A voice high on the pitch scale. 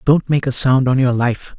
No: low, 130 Hz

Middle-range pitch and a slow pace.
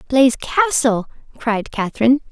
No: very high, 250 Hz; slow, 105 wpm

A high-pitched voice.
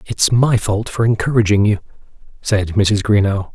No: low, 105 Hz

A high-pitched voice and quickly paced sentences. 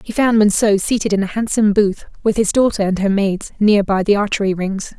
Yes: high, 205 Hz; fast, 230 wpm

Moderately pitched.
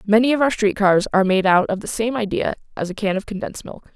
No: high, 210 Hz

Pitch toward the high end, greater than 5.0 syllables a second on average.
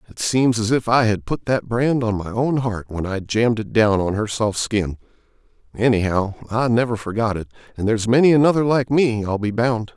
No: low, 115 Hz; 5.3 syllables/s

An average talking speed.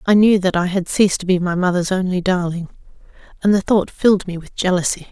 No: fast, 225 wpm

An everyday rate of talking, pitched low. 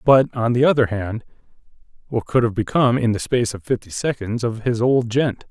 Yes: average, 185 wpm; low, 115 Hz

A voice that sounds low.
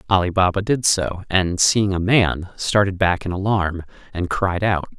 Yes: very low, 95 Hz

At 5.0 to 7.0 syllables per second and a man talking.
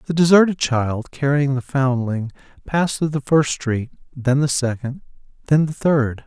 No: 4.4 syllables/s; male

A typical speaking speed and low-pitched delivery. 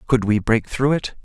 No: fast, 240 wpm; low, 120 Hz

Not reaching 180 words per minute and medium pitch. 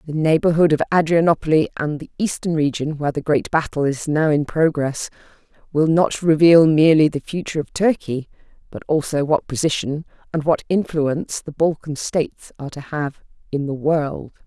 Yes: average, 165 wpm; medium, 155 Hz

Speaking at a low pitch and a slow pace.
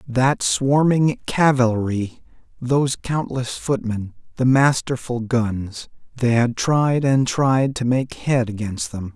Yes: low, 125 Hz; slow, 120 wpm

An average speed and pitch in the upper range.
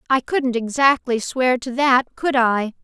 Yes: average, 170 wpm; very high, 250 Hz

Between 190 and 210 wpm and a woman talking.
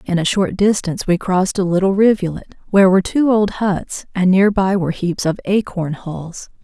Yes: average, 200 wpm; female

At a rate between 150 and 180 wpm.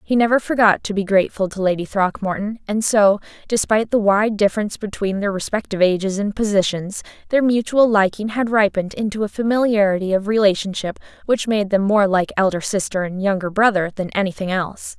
Yes: average, 175 wpm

